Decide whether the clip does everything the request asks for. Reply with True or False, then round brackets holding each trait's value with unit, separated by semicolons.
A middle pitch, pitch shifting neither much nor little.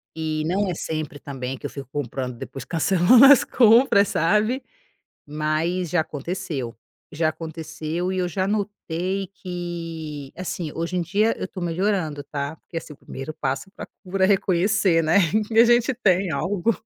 True (170 Hz; 4.1 semitones)